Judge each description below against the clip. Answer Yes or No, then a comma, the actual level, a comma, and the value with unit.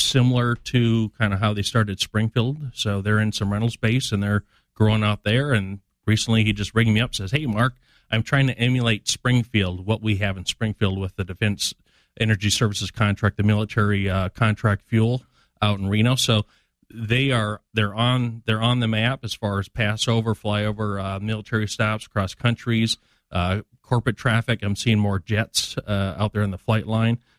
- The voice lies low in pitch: Yes, low, 110 Hz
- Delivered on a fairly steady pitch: Yes, narrow, 2.1 semitones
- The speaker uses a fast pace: No, average, 190 wpm